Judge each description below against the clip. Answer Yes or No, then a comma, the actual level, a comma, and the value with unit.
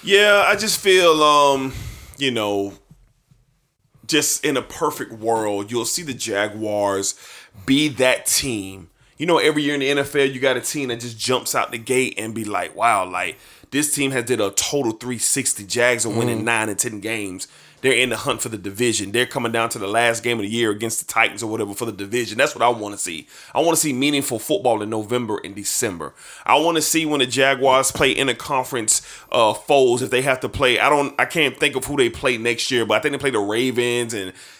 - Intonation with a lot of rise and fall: No, average, 4.0 semitones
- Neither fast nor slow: No, fast, 230 wpm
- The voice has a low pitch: Yes, low, 120 Hz